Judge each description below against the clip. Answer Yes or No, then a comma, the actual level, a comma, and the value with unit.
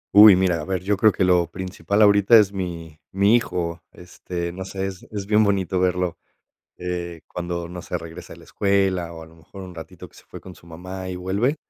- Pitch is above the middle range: No, very low, 90 Hz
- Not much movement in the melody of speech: Yes, narrow, 2.2 semitones